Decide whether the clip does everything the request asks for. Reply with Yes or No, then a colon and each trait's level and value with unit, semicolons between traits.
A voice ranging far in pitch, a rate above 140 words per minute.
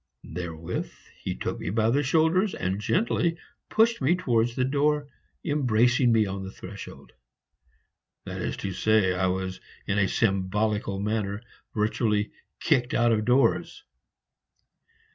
No: wide, 5.7 semitones; slow, 135 wpm